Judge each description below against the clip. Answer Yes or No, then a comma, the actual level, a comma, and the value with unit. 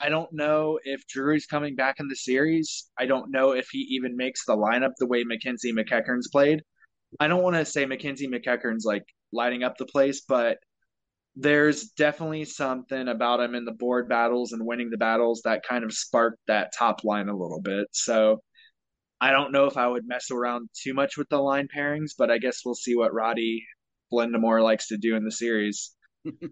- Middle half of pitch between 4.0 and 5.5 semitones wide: No, average, 3.3 semitones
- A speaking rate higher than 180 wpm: Yes, fast, 205 wpm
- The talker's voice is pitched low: Yes, low, 125 Hz